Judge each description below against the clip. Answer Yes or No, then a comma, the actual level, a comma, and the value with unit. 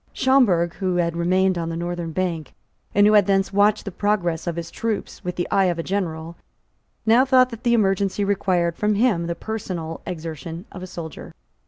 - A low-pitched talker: No, medium, 185 Hz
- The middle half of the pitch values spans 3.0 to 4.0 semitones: Yes, average, 3.3 semitones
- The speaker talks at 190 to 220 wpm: Yes, average, 195 wpm